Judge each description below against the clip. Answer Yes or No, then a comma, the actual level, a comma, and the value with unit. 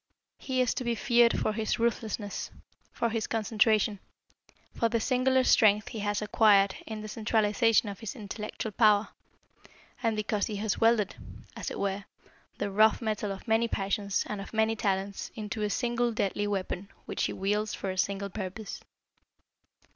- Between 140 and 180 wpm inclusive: Yes, average, 165 wpm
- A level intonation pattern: Yes, narrow, 2.0 semitones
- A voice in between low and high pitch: No, high, 215 Hz